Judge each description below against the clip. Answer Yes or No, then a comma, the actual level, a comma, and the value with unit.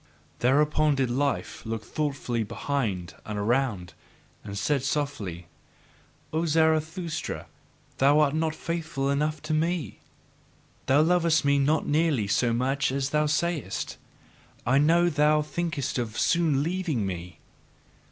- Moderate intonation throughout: Yes, average, 4.2 semitones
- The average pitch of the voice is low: No, medium, 145 Hz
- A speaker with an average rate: No, slow, 125 wpm